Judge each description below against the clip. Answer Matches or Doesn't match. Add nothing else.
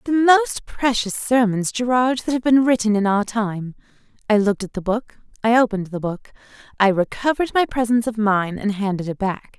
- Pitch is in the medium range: Doesn't match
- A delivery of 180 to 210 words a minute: Matches